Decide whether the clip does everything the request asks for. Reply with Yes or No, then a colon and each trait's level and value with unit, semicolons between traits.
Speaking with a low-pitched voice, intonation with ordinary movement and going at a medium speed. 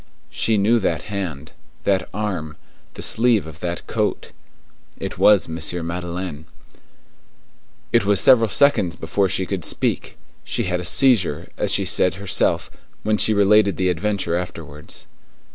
Yes: very low, 95 Hz; average, 3.7 semitones; average, 145 wpm